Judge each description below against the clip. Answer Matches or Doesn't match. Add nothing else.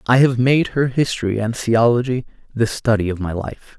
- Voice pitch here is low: Matches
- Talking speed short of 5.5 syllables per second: Matches